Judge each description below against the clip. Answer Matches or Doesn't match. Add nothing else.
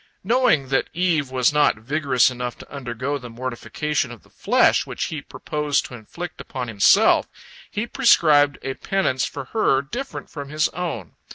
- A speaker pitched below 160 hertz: Matches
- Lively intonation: Doesn't match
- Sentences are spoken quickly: Doesn't match